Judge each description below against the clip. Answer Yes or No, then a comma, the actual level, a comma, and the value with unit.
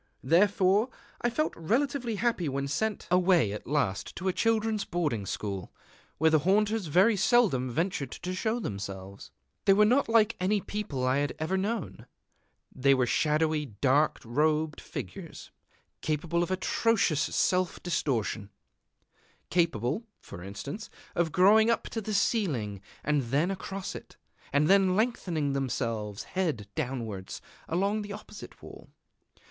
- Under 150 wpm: Yes, average, 140 wpm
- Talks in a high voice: No, medium, 170 Hz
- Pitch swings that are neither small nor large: No, wide, 7.2 semitones